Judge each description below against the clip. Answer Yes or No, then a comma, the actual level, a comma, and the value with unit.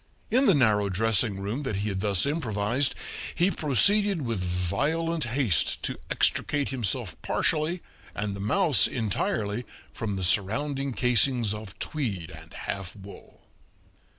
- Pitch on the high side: No, low, 115 Hz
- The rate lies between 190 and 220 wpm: No, slow, 135 wpm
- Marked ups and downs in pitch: Yes, wide, 6.3 semitones